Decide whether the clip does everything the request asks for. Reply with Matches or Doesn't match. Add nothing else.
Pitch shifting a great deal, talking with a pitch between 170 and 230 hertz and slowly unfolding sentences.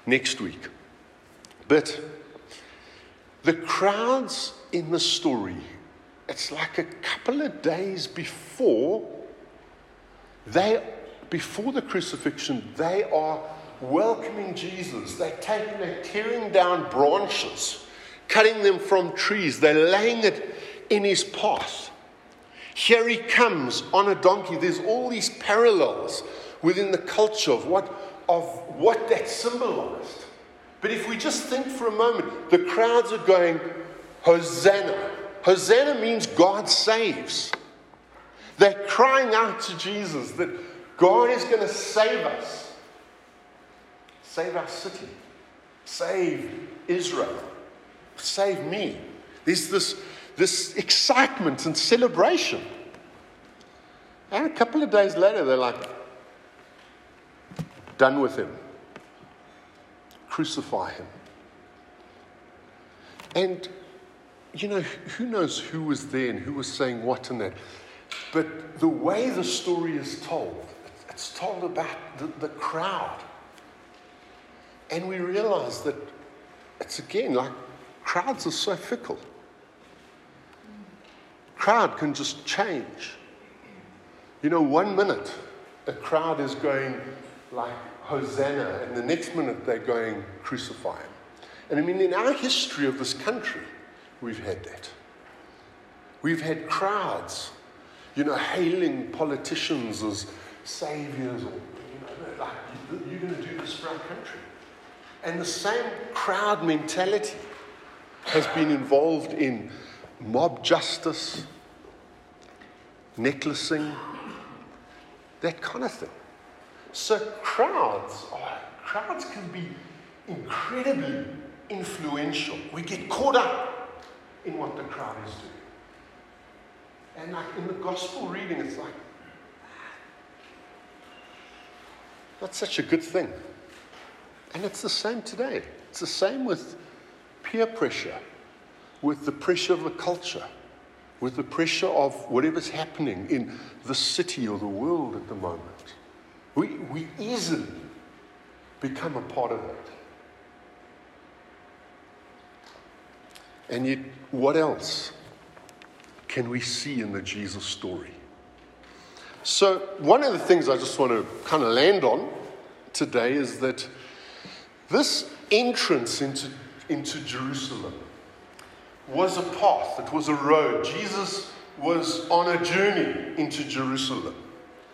Matches